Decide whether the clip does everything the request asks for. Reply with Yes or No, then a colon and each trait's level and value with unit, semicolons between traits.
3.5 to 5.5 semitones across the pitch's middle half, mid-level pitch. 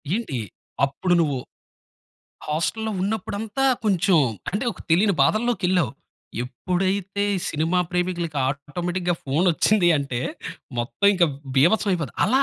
Yes: average, 4.4 semitones; medium, 180 Hz